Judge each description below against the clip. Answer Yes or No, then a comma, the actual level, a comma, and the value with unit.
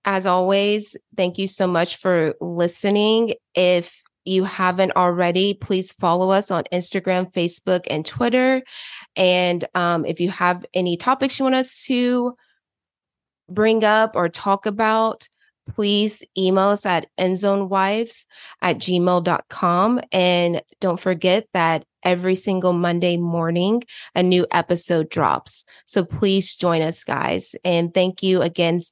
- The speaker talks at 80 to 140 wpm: Yes, slow, 135 wpm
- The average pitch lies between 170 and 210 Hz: Yes, medium, 185 Hz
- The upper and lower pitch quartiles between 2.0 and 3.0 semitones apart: Yes, narrow, 2.4 semitones